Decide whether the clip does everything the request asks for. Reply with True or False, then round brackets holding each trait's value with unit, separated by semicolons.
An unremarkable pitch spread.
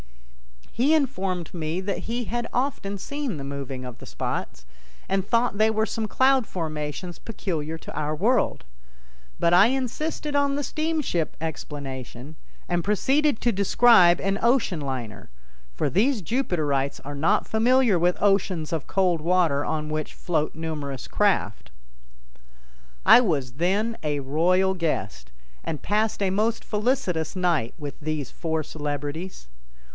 False (6.7 semitones)